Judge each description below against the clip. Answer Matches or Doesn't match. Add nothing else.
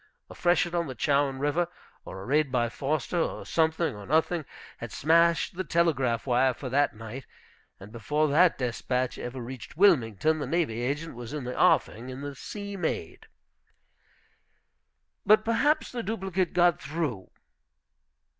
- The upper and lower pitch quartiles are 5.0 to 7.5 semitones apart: Matches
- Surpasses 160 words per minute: Doesn't match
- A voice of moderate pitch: Matches